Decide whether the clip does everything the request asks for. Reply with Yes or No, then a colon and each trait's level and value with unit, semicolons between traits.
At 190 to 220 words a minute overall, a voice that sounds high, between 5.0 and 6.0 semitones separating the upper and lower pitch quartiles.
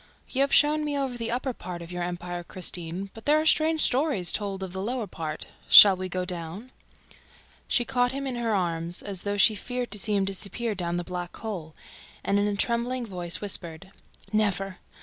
Yes: fast, 205 wpm; high, 200 Hz; wide, 5.5 semitones